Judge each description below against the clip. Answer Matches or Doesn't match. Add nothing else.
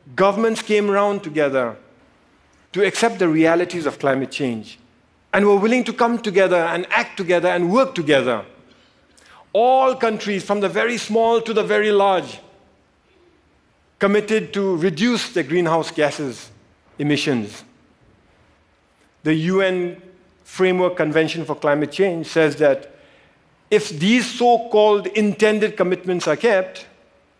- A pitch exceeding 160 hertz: Matches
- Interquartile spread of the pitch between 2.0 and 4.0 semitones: Doesn't match